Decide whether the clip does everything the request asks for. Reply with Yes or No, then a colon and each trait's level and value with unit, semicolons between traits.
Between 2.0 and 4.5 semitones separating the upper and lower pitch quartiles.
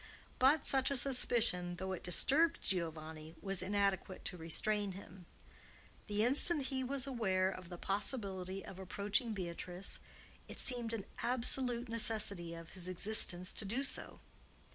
No: average, 5.1 semitones